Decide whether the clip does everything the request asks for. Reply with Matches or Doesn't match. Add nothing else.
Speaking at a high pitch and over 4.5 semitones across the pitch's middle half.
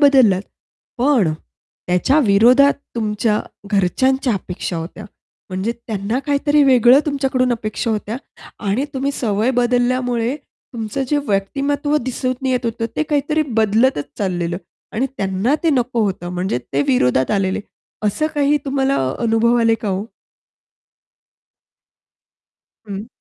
Matches